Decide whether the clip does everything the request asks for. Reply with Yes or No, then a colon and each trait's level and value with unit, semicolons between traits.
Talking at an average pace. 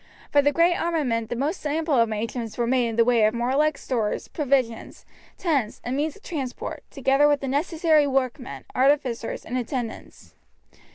Yes: average, 165 wpm